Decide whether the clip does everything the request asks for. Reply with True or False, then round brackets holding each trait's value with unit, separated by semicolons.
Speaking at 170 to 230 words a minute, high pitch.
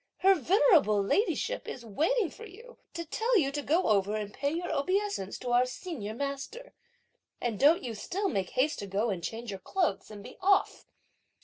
True (190 wpm; 280 Hz)